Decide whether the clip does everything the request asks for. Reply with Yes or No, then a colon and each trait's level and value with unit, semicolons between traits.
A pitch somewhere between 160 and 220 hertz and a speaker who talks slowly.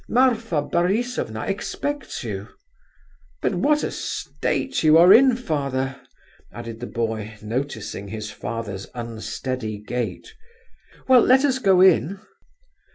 No: medium, 140 Hz; slow, 115 wpm